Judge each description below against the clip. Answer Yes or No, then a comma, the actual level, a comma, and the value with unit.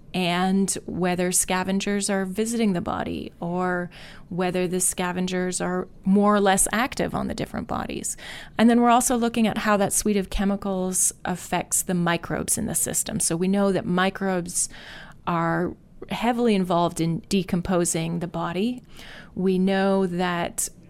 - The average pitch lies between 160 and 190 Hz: Yes, medium, 185 Hz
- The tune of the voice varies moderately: No, narrow, 2.1 semitones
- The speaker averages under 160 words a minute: Yes, average, 150 wpm